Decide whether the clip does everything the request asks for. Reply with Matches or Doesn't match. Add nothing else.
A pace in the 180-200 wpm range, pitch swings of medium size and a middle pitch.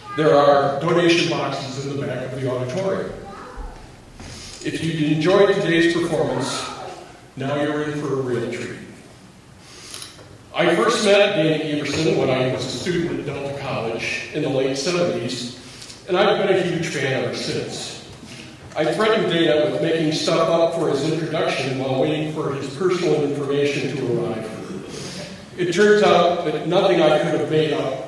Doesn't match